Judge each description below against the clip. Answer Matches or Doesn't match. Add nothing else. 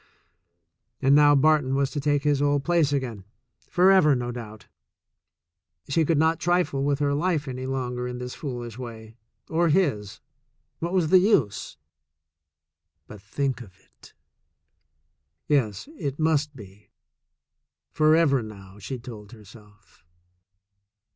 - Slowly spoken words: Matches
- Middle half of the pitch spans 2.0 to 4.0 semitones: Doesn't match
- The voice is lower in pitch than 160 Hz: Matches